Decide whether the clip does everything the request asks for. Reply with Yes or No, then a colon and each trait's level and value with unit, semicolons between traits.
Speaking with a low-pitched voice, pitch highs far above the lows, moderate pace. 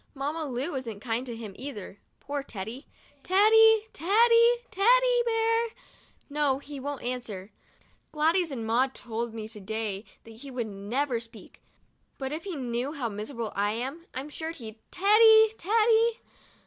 No: very high, 275 Hz; wide, 8.8 semitones; average, 160 wpm